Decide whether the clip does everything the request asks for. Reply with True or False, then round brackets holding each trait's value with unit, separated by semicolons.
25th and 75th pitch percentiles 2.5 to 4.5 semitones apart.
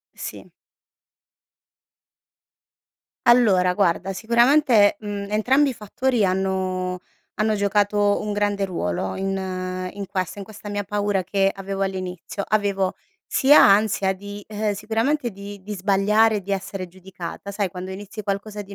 False (1.9 semitones)